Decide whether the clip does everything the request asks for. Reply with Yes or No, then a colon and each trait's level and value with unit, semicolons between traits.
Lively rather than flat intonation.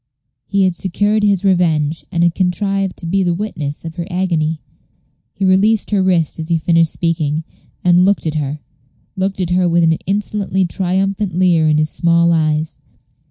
No: average, 2.8 semitones